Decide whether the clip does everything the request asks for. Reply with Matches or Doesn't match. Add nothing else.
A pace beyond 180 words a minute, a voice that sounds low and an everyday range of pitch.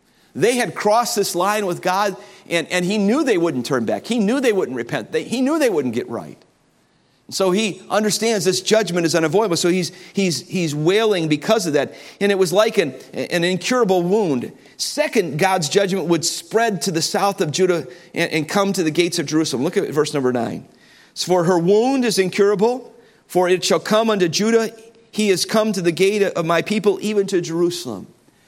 Doesn't match